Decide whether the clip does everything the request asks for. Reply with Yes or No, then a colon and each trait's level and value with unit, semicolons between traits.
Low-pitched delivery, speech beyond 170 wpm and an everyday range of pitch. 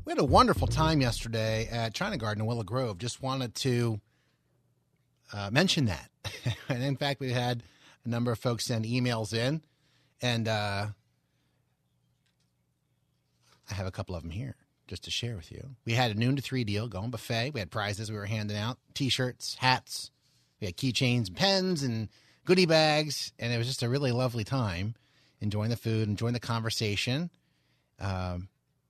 Yes: low, 115 Hz; average, 180 wpm; average, 3.6 semitones